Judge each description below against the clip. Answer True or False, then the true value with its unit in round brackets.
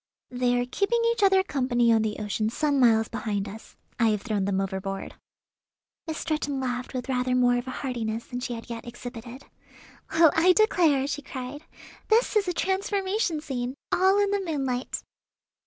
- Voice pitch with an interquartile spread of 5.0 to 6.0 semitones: True (5.6 semitones)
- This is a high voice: True (255 Hz)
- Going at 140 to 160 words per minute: False (170 wpm)